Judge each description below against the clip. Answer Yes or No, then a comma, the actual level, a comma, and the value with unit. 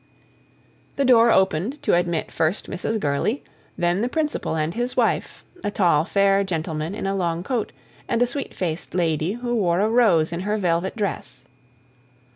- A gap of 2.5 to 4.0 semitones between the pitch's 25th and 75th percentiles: No, average, 5.2 semitones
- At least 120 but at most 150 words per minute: No, average, 170 wpm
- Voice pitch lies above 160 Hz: Yes, high, 190 Hz